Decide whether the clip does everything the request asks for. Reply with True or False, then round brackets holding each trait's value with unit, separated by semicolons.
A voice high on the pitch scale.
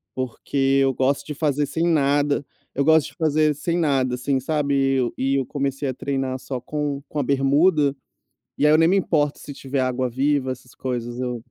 False (140 Hz)